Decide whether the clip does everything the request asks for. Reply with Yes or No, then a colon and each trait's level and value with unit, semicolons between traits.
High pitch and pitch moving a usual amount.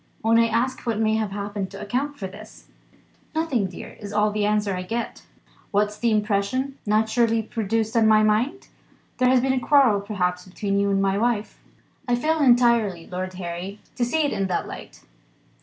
Yes: high, 215 Hz; average, 3.2 semitones